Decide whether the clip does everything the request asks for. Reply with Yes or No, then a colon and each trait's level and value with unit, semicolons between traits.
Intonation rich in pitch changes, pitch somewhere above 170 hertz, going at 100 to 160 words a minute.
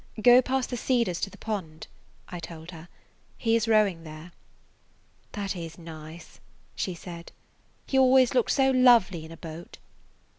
Yes: wide, 6.7 semitones; medium, 185 Hz; average, 155 wpm